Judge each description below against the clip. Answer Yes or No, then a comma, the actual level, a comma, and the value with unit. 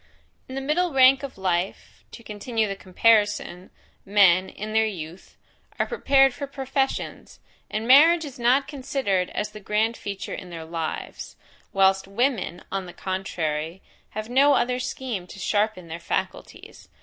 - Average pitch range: No, wide, 5.8 semitones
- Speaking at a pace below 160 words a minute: Yes, average, 150 wpm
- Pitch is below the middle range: No, high, 215 Hz